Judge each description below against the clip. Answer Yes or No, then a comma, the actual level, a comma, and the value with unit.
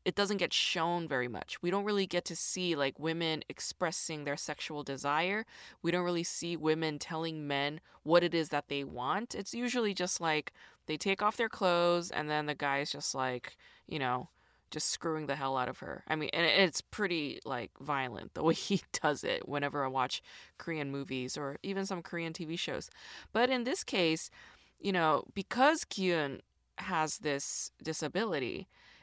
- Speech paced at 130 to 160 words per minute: No, average, 185 wpm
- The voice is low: No, medium, 165 Hz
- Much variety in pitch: No, average, 4.3 semitones